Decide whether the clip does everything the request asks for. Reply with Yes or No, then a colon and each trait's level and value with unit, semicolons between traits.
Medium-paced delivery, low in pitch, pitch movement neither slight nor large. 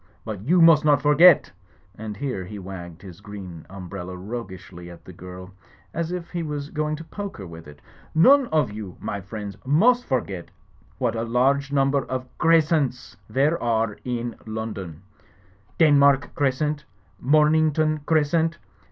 No: average, 155 wpm; low, 130 Hz; wide, 7.5 semitones